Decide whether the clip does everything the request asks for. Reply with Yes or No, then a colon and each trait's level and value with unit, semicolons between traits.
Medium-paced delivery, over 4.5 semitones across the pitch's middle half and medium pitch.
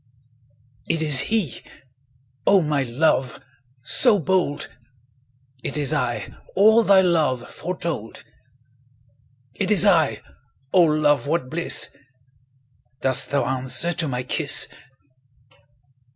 No: slow, 95 wpm; average, 4.9 semitones; medium, 150 Hz